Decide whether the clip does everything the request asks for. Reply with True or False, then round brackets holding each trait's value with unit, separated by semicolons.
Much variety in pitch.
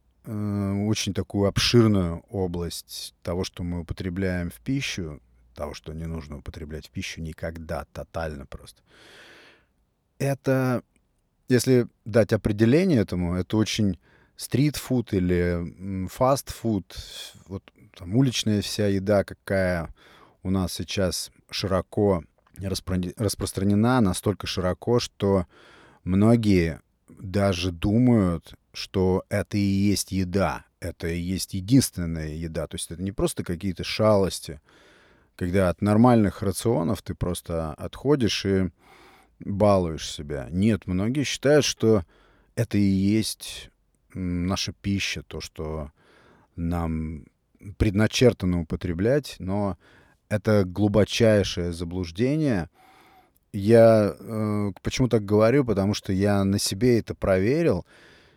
False (3.6 semitones)